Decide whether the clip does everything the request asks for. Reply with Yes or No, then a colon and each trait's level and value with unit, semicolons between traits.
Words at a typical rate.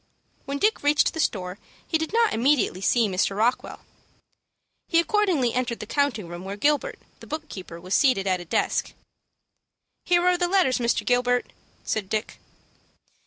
Yes: average, 165 wpm